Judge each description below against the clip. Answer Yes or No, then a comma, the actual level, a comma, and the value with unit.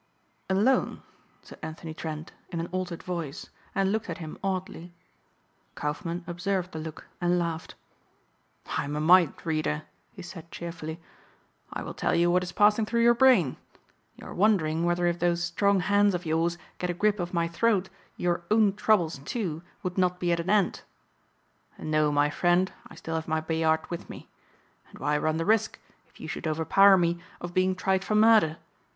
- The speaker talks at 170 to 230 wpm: Yes, average, 180 wpm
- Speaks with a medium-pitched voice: Yes, medium, 175 Hz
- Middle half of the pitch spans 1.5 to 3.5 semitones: Yes, average, 3.0 semitones